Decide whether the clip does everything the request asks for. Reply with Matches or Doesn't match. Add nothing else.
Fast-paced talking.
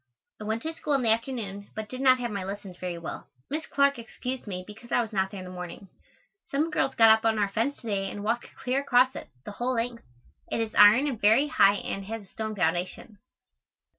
Matches